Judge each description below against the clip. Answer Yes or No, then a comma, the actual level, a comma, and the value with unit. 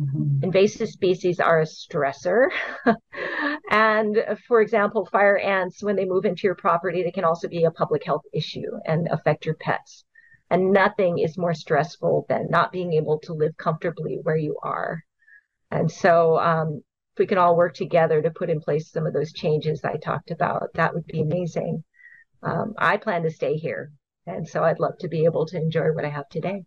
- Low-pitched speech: No, medium, 170 Hz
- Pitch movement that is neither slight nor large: Yes, average, 3.5 semitones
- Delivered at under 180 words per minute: No, average, 195 wpm